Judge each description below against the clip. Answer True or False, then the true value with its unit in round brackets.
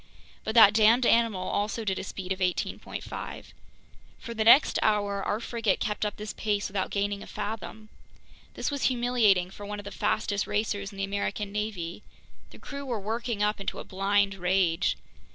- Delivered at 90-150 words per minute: False (180 wpm)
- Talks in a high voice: True (205 Hz)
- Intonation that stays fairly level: True (1.9 semitones)